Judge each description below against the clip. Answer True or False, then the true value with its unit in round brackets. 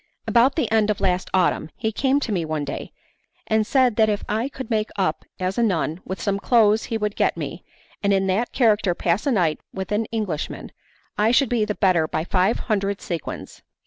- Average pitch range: True (3.4 semitones)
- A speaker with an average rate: False (210 wpm)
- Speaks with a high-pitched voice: True (210 Hz)